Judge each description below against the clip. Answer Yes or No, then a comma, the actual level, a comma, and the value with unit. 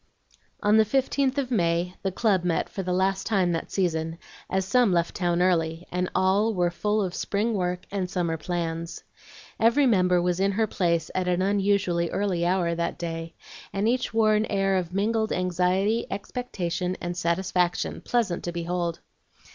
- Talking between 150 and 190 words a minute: Yes, average, 170 wpm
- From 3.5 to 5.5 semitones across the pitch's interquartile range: No, average, 2.8 semitones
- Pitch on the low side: No, medium, 185 Hz